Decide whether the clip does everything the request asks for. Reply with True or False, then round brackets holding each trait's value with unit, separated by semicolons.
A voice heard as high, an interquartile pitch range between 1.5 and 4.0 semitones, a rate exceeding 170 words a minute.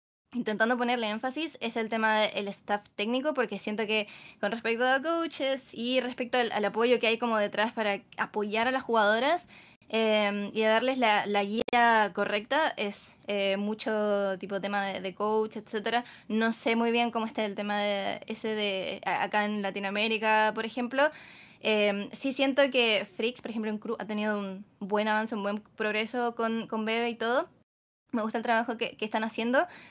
True (220 Hz; 2.4 semitones; 185 wpm)